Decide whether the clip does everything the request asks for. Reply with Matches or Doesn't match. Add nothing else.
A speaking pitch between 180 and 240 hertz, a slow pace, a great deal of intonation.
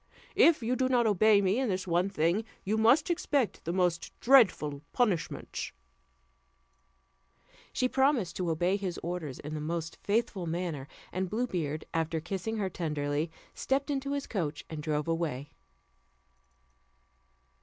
Doesn't match